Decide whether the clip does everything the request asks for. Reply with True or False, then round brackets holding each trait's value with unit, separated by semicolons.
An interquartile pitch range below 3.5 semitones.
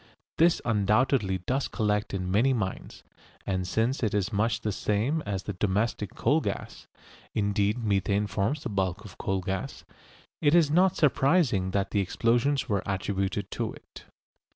False (4.3 semitones)